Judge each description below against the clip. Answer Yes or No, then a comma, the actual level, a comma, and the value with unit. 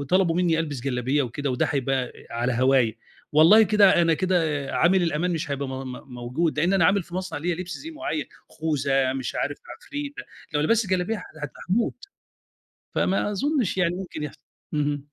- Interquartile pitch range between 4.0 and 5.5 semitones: Yes, average, 5.2 semitones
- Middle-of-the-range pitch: Yes, medium, 160 Hz